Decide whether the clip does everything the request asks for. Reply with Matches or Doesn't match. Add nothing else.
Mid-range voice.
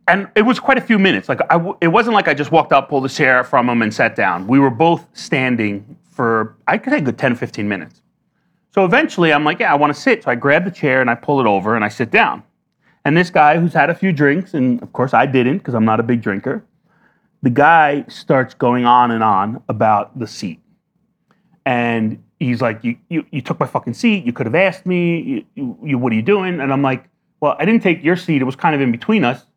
Matches